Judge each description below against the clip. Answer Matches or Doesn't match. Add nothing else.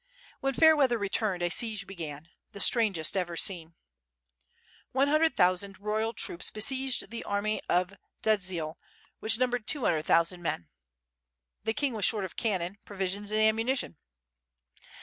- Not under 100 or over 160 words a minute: Matches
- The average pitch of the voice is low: Doesn't match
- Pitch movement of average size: Matches